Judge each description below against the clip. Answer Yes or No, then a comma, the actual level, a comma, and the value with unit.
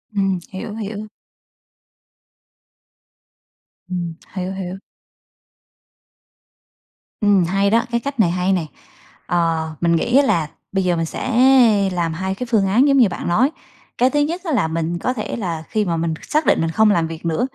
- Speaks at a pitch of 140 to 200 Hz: Yes, high, 190 Hz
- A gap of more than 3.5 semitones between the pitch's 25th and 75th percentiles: Yes, average, 5.2 semitones